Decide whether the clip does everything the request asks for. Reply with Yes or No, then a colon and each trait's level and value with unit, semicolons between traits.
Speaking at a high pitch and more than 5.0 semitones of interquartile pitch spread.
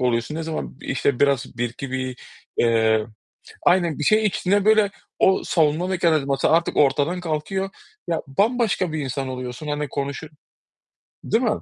No: medium, 150 Hz; wide, 5.4 semitones